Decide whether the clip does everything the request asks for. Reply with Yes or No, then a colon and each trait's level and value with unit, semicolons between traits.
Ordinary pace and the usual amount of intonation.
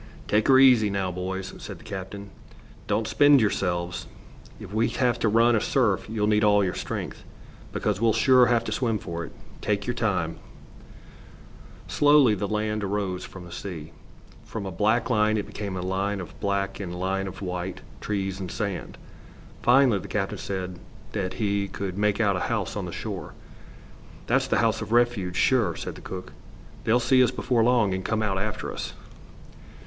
Yes: average, 185 wpm; average, 3.0 semitones